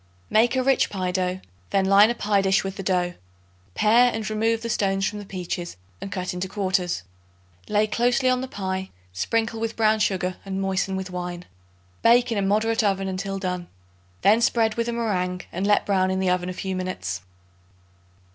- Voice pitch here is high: Yes, high, 195 Hz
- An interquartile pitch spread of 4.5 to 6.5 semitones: No, average, 3.2 semitones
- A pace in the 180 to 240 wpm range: Yes, average, 195 wpm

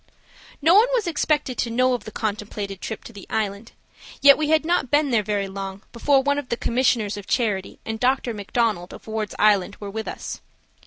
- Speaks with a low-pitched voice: No, high, 225 Hz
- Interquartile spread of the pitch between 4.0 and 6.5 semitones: Yes, average, 4.7 semitones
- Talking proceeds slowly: No, fast, 205 wpm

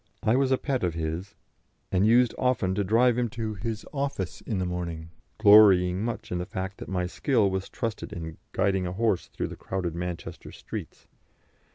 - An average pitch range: Yes, average, 4.4 semitones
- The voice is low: Yes, low, 100 Hz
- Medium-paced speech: Yes, average, 190 wpm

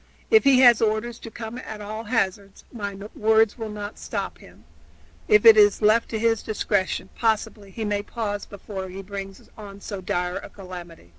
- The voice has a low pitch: No, high, 210 Hz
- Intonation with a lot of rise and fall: No, narrow, 2.5 semitones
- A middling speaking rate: Yes, average, 180 wpm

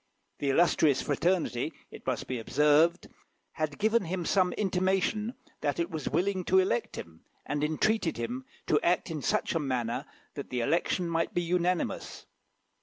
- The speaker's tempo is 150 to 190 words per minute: Yes, average, 160 wpm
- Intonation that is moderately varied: Yes, average, 4.2 semitones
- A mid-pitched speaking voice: Yes, medium, 170 Hz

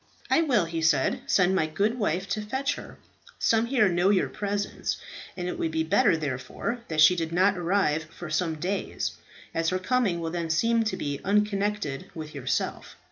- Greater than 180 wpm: Yes, average, 190 wpm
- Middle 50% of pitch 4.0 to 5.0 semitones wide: Yes, average, 4.5 semitones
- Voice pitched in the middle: Yes, medium, 180 Hz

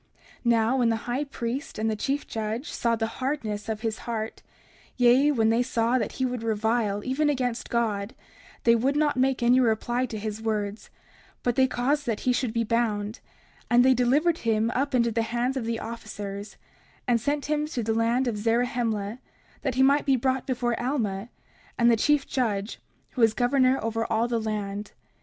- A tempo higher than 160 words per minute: Yes, average, 195 wpm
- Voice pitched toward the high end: Yes, high, 235 Hz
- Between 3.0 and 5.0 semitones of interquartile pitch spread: No, narrow, 2.6 semitones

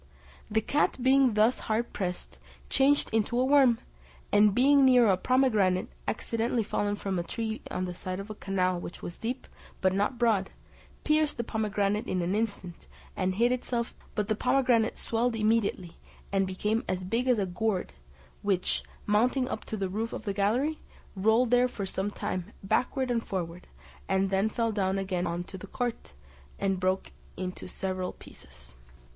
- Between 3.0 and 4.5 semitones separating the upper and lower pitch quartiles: Yes, average, 4.1 semitones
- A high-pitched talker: Yes, high, 210 Hz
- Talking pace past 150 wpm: Yes, average, 170 wpm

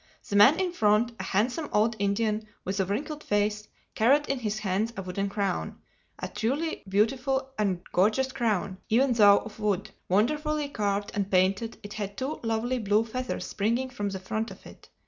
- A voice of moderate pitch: No, high, 215 Hz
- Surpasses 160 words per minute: Yes, average, 175 wpm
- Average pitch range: Yes, average, 4.0 semitones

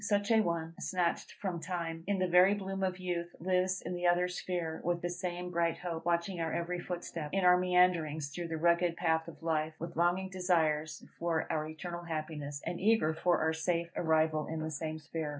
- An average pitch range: No, narrow, 2.0 semitones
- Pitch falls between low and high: Yes, medium, 170 Hz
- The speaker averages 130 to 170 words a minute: No, fast, 205 wpm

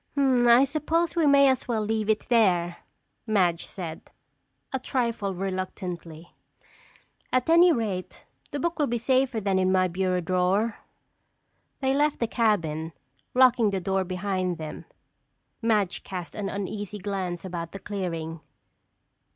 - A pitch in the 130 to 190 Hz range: No, high, 200 Hz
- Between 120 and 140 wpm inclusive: Yes, slow, 135 wpm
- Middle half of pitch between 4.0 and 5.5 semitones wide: Yes, average, 5.1 semitones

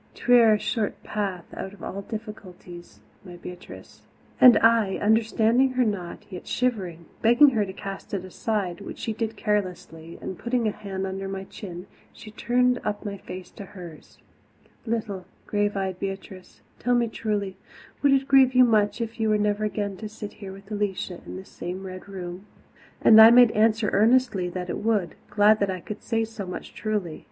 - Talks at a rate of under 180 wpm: No, average, 185 wpm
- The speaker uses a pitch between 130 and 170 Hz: No, high, 205 Hz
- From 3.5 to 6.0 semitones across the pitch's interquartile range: No, average, 2.9 semitones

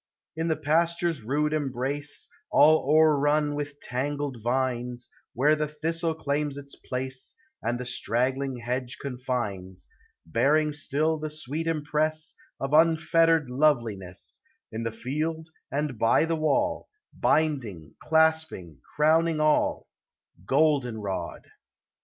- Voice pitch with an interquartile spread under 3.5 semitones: No, average, 3.9 semitones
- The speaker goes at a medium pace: No, slow, 115 wpm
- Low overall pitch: No, medium, 145 Hz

